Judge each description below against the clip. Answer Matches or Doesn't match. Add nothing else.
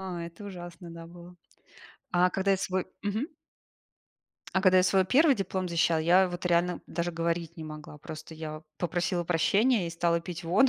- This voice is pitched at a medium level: Matches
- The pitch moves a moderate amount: Doesn't match